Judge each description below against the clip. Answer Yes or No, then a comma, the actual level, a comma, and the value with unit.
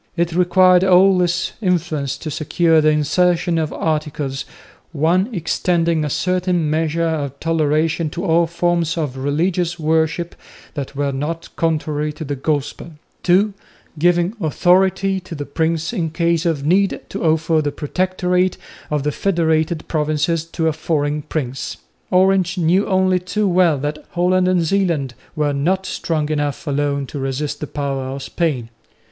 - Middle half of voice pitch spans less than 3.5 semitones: Yes, average, 3.1 semitones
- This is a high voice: No, medium, 165 Hz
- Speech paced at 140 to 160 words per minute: Yes, average, 150 wpm